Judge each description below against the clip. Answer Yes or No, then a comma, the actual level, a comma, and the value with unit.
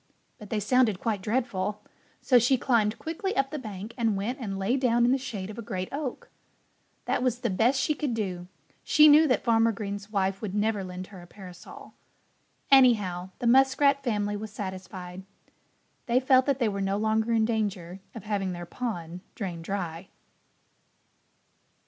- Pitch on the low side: No, high, 215 Hz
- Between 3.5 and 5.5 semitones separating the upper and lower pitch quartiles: Yes, average, 4.4 semitones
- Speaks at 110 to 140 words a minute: No, average, 175 wpm